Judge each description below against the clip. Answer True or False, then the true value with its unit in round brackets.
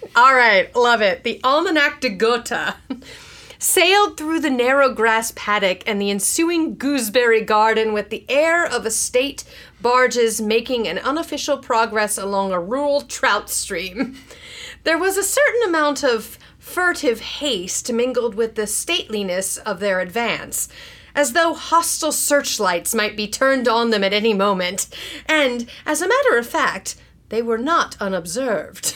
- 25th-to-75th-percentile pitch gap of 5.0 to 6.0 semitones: True (5.4 semitones)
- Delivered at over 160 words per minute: False (150 wpm)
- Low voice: False (245 Hz)